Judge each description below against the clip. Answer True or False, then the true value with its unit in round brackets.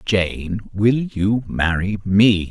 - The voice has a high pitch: False (100 Hz)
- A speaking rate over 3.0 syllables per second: False (2.6 syllables/s)